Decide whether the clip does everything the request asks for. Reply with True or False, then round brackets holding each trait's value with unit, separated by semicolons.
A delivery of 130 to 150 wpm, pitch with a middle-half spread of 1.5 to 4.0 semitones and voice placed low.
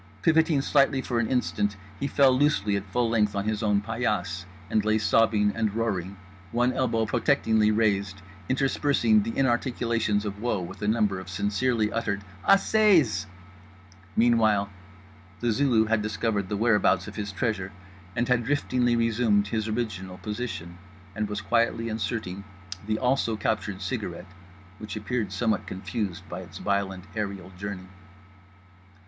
True (140 wpm; 3.1 semitones; 110 Hz)